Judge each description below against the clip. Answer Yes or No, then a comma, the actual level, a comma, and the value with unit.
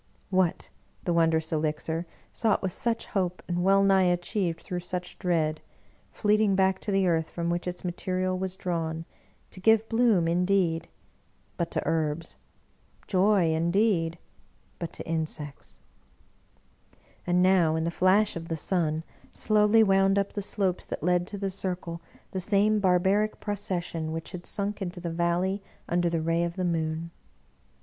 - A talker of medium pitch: Yes, medium, 180 Hz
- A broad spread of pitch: No, average, 2.7 semitones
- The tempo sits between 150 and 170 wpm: Yes, average, 165 wpm